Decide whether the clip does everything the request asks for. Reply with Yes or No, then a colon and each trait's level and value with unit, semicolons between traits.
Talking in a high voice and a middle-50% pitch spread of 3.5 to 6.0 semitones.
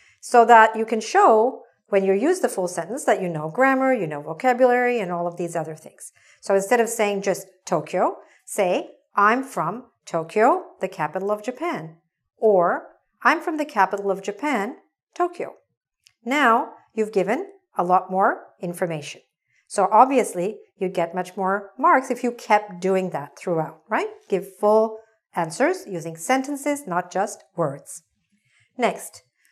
Yes: high, 210 Hz; wide, 5.5 semitones